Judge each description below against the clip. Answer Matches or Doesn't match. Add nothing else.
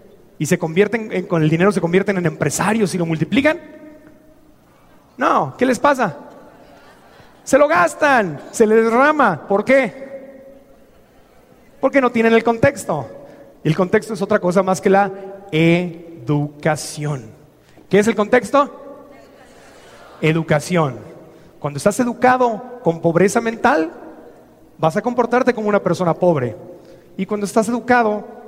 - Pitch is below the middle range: Doesn't match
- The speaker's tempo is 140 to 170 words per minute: Doesn't match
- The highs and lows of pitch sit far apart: Matches